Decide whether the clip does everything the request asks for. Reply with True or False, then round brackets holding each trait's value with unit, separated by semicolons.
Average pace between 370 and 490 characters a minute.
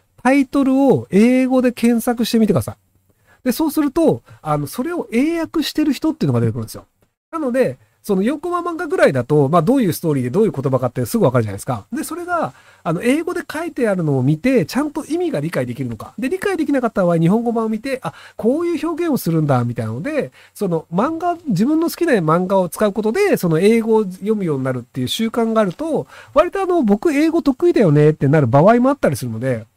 True (465 characters per minute)